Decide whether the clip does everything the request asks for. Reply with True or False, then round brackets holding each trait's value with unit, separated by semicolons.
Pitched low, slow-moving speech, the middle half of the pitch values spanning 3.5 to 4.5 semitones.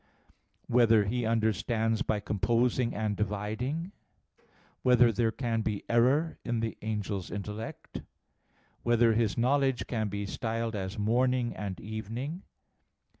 False (115 Hz; 130 wpm; 2.5 semitones)